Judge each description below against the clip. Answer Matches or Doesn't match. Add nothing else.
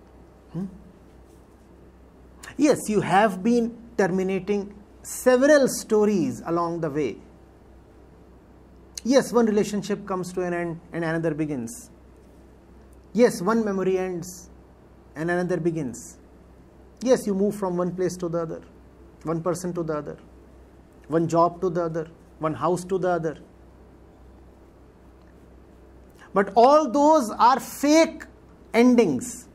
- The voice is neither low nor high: Matches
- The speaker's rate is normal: Doesn't match